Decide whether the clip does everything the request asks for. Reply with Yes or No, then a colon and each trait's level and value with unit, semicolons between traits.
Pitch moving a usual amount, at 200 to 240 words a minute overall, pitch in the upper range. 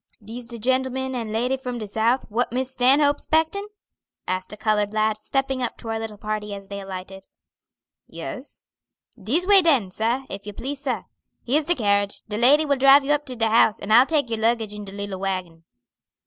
Yes: average, 4.3 semitones; fast, 205 wpm; high, 230 Hz